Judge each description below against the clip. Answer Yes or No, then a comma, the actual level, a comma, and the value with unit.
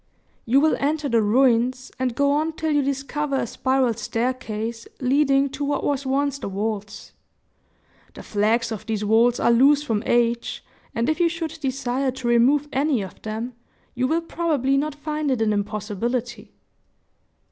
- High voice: Yes, very high, 260 Hz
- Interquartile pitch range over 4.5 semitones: No, average, 3.8 semitones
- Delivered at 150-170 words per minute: Yes, average, 165 wpm